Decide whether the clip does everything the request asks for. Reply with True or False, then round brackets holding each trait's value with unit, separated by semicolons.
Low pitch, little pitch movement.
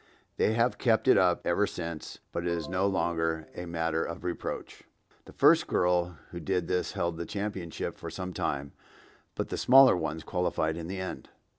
True (85 Hz; 2.2 semitones)